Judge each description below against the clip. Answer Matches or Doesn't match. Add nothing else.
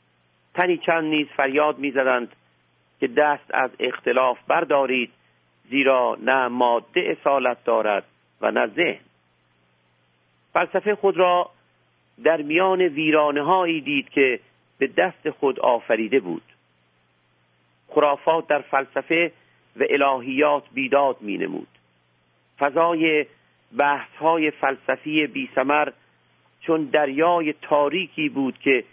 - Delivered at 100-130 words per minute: Matches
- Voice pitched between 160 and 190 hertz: Doesn't match